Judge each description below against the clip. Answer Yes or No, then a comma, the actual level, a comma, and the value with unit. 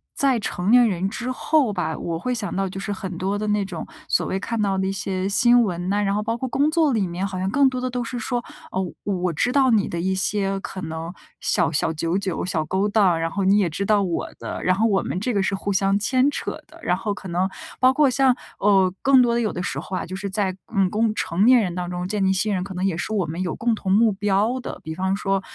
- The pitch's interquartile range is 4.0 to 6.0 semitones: No, average, 3.6 semitones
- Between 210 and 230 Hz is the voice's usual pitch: No, high, 195 Hz